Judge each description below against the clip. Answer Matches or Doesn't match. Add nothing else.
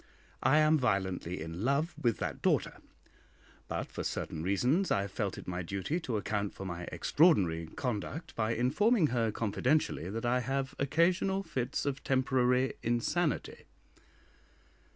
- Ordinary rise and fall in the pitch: Doesn't match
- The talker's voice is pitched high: Doesn't match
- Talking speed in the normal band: Matches